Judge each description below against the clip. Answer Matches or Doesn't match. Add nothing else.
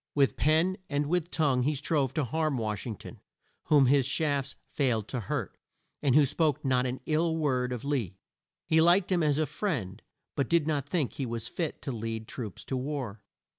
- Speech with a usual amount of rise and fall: Matches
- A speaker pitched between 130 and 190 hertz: Matches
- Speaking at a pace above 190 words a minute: Matches